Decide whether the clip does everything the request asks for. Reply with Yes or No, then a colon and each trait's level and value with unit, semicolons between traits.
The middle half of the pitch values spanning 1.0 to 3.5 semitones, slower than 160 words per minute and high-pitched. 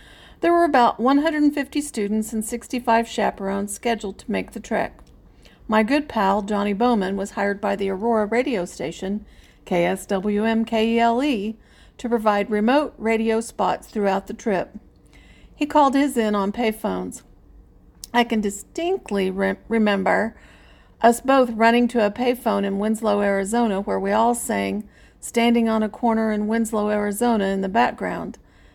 Yes: average, 2.8 semitones; average, 140 wpm; high, 220 Hz